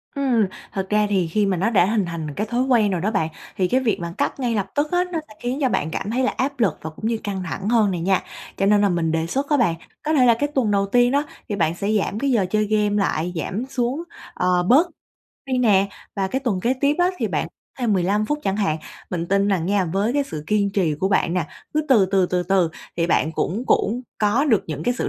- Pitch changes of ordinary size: Yes, average, 5.0 semitones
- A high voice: Yes, high, 205 Hz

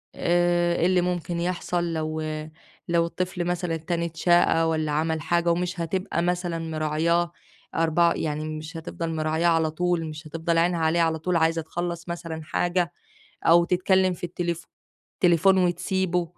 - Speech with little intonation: Yes, narrow, 1.4 semitones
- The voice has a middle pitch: Yes, medium, 170 Hz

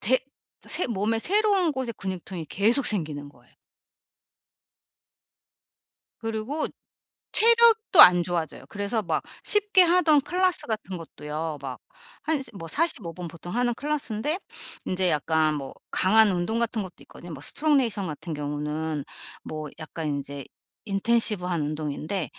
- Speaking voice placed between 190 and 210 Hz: Yes, high, 195 Hz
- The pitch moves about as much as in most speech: No, wide, 8.6 semitones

